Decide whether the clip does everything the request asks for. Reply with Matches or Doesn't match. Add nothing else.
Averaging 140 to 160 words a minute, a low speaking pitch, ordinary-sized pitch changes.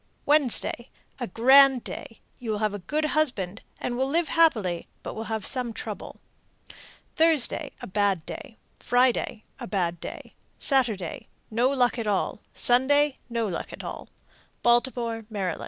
Doesn't match